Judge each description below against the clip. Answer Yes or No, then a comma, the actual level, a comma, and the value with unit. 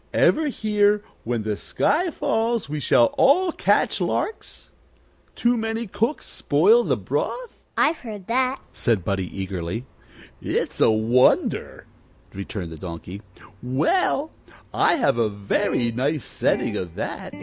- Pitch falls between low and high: Yes, medium, 150 Hz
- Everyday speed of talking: No, slow, 130 wpm